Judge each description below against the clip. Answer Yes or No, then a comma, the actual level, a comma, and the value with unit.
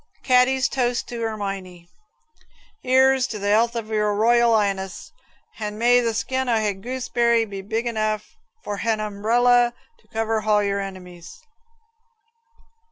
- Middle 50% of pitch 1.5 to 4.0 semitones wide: Yes, average, 2.9 semitones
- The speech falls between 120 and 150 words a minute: Yes, average, 140 wpm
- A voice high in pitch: Yes, high, 220 Hz